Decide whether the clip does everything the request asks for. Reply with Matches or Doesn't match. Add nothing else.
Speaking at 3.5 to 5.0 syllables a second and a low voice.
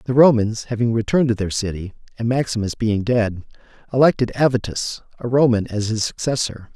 Doesn't match